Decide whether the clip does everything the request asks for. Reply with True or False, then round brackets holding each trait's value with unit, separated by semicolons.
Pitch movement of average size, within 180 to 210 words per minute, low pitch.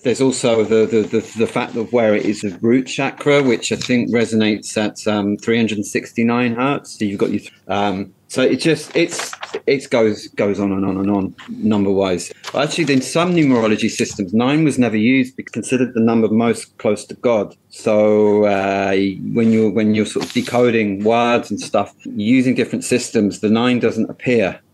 True (3.2 semitones; 185 wpm; 115 Hz)